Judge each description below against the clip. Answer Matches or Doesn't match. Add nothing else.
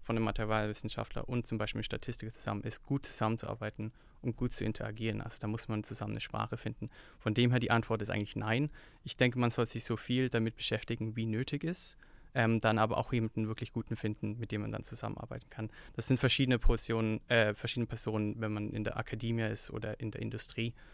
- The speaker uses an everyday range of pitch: Doesn't match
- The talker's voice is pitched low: Matches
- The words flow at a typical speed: Doesn't match